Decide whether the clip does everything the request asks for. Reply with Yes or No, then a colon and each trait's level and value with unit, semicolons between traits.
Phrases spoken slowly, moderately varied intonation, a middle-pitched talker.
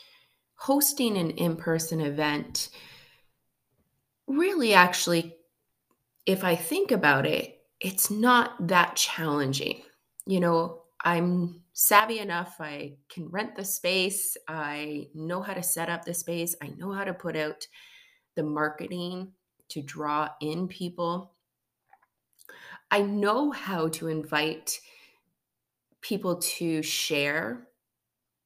Yes: slow, 115 wpm; average, 4.0 semitones; medium, 175 Hz